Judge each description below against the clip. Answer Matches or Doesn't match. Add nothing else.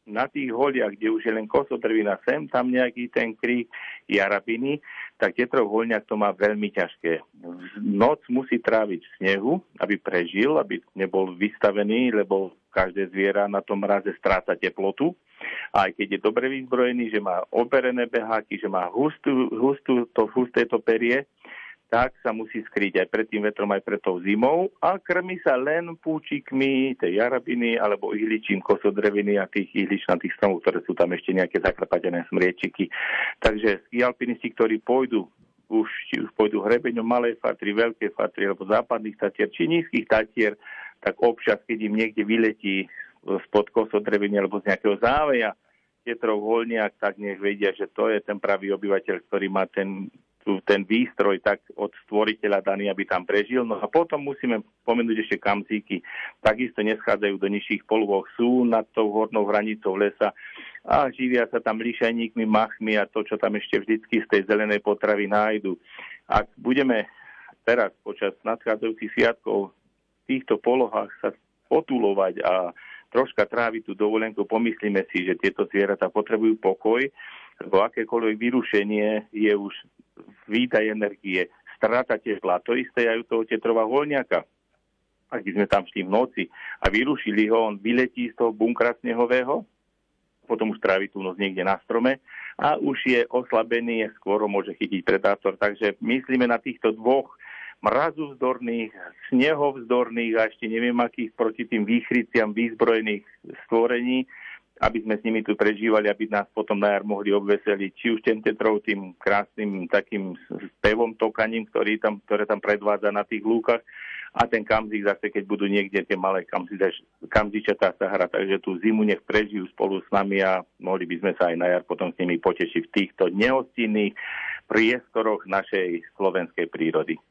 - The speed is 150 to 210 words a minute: Matches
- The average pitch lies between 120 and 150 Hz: Doesn't match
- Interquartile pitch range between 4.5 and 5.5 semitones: Doesn't match